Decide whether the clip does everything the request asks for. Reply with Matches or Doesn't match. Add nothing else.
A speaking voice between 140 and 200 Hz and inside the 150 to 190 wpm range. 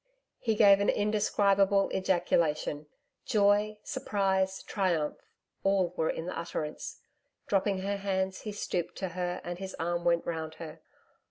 Doesn't match